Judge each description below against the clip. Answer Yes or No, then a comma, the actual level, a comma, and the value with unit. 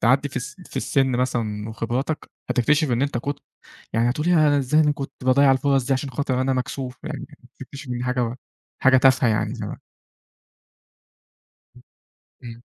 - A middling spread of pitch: No, narrow, 2.3 semitones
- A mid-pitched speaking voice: No, low, 130 Hz